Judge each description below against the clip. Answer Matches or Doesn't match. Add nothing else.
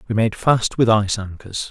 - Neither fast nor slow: Doesn't match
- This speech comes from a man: Matches